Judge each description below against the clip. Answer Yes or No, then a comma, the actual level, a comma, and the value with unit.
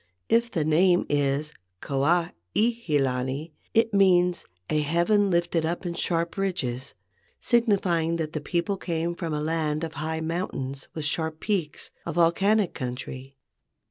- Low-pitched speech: No, medium, 165 Hz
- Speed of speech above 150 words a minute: No, average, 145 wpm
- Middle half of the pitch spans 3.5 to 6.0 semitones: No, average, 3.1 semitones